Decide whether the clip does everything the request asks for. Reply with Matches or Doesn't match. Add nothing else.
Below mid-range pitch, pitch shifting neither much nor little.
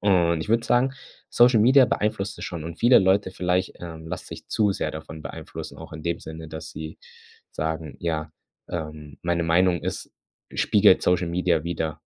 Matches